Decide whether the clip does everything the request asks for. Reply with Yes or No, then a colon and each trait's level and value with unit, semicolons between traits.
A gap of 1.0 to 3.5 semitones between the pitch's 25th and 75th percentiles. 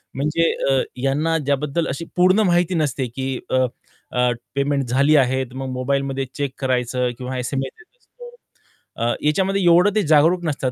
No: average, 4.3 semitones